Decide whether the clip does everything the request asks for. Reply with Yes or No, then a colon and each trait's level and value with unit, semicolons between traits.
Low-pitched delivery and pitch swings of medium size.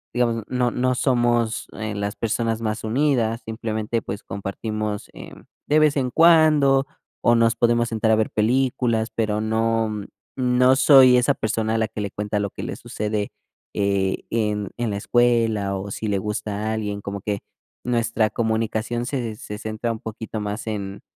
No: low, 110 Hz; narrow, 2.3 semitones